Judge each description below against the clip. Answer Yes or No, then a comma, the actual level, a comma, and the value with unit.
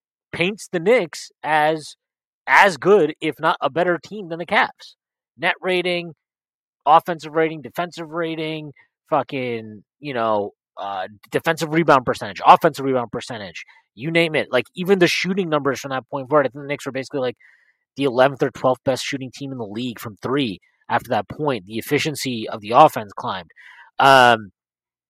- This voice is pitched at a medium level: Yes, medium, 145 Hz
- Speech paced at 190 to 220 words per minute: No, average, 165 wpm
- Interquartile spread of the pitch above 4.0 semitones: Yes, average, 5.1 semitones